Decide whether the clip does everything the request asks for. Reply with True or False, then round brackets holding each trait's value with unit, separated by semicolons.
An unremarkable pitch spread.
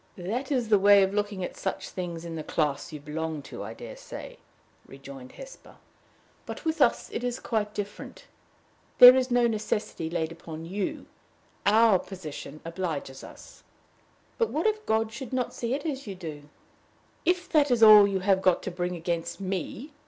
False (6.6 semitones)